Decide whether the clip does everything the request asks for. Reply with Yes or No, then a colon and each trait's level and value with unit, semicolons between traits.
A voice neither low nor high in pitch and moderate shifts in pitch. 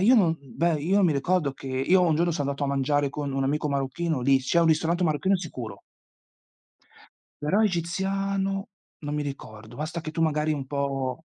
Yes: medium, 155 Hz; average, 3.8 semitones